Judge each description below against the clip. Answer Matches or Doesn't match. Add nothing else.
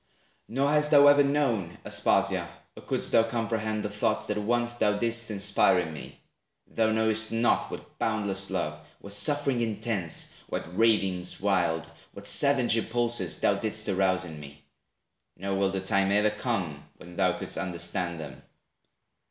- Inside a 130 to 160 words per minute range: Matches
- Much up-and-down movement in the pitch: Doesn't match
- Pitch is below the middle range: Matches